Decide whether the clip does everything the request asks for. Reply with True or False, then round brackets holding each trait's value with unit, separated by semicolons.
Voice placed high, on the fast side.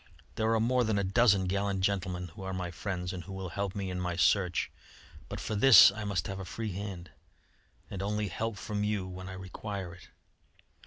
False (95 Hz; 210 wpm)